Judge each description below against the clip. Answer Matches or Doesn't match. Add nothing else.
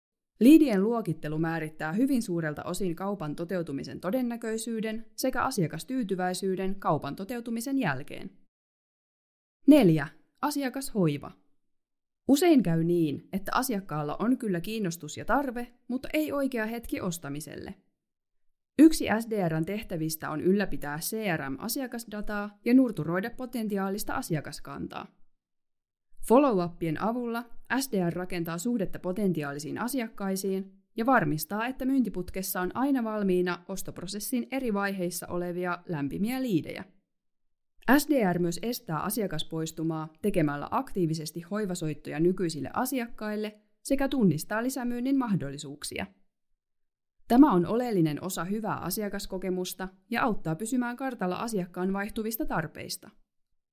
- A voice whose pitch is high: Matches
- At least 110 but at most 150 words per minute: Doesn't match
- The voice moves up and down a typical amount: Doesn't match